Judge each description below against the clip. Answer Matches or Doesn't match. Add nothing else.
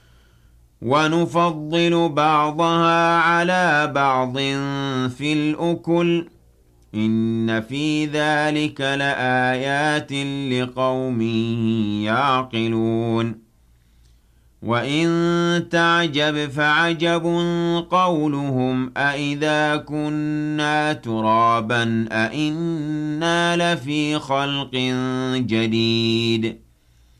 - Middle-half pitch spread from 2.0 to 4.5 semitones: Doesn't match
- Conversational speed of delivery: Doesn't match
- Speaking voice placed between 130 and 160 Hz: Matches